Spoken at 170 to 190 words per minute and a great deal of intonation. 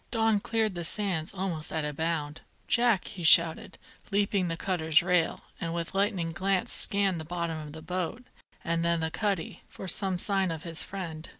No: average, 185 wpm; average, 3.2 semitones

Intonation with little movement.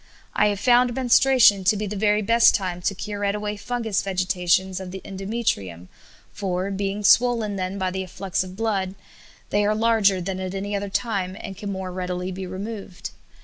Yes: narrow, 2.1 semitones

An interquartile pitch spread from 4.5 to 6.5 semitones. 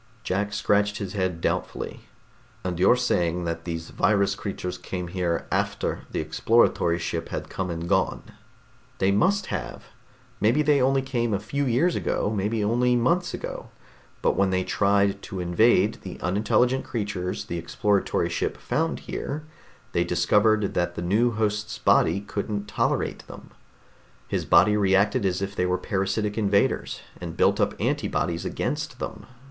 No: average, 3.6 semitones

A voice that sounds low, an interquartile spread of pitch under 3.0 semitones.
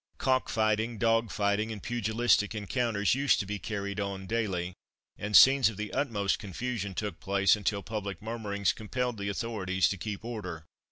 Yes: low, 105 Hz; narrow, 2.4 semitones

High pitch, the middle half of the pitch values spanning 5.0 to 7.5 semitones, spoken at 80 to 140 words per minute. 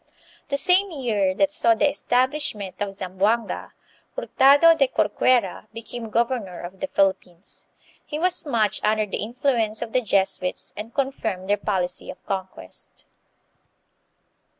Yes: high, 220 Hz; wide, 5.6 semitones; slow, 135 wpm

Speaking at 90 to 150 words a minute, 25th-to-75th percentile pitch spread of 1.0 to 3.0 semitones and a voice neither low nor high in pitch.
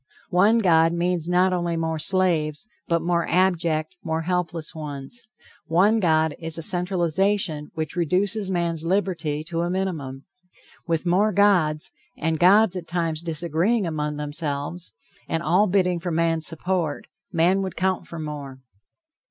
Yes: average, 145 wpm; narrow, 2.6 semitones; medium, 170 Hz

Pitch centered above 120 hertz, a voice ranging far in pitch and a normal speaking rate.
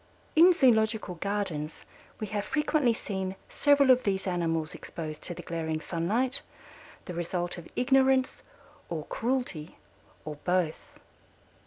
No: high, 190 Hz; wide, 7.1 semitones; slow, 125 wpm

